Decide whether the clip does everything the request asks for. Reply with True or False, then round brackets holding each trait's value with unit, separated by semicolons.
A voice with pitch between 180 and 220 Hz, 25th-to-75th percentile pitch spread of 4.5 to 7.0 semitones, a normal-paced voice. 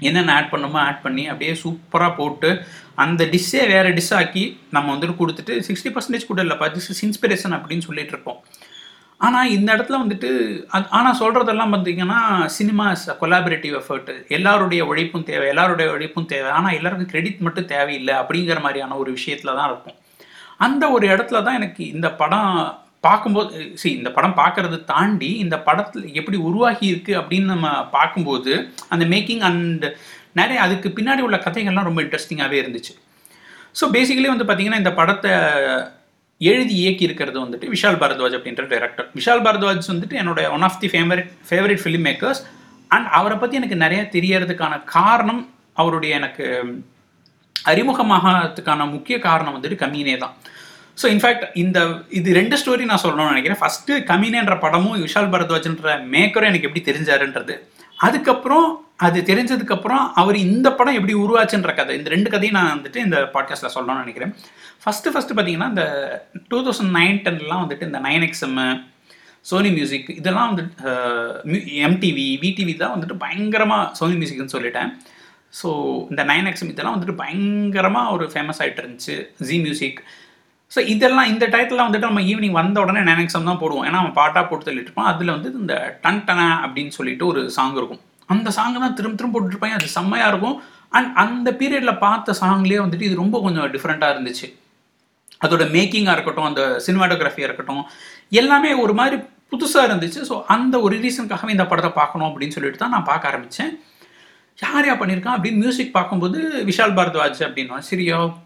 False (185 Hz; 5.1 semitones; 155 wpm)